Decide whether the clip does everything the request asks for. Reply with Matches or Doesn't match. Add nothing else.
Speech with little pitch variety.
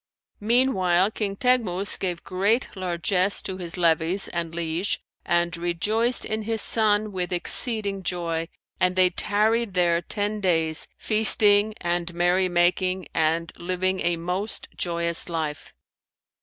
Doesn't match